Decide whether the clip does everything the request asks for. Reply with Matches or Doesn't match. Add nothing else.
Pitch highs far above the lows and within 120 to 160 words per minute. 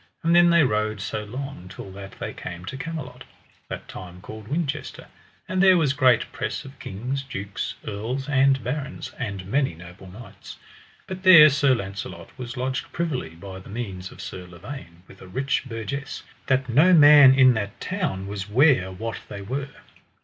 Doesn't match